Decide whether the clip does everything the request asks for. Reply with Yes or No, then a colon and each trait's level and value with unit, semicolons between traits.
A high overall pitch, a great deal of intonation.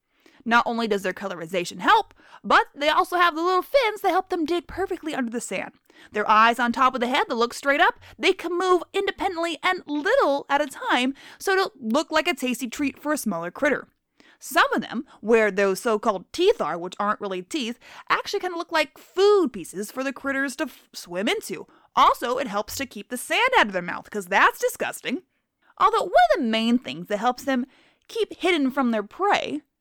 Yes: very high, 280 Hz; wide, 7.3 semitones